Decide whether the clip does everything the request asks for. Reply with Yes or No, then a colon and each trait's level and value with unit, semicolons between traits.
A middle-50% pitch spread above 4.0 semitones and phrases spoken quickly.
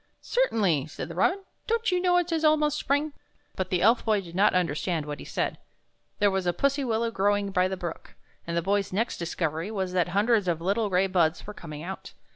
Yes: average, 5.0 semitones; fast, 235 wpm